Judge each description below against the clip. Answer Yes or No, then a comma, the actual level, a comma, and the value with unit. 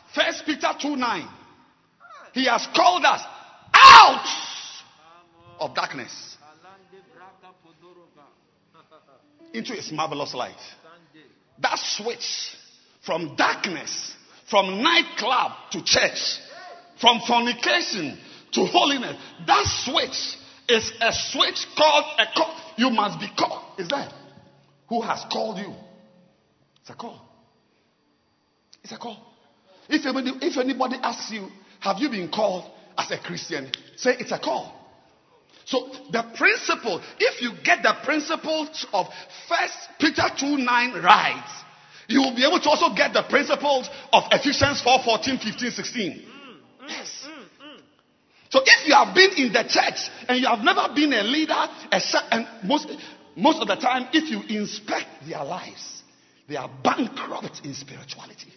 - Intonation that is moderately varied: No, wide, 5.7 semitones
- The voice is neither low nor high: No, very high, 255 Hz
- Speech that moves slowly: Yes, slow, 130 wpm